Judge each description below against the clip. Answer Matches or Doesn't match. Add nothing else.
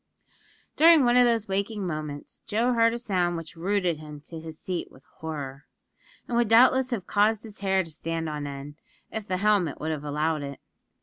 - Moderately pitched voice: Matches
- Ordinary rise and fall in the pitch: Doesn't match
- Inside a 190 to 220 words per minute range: Matches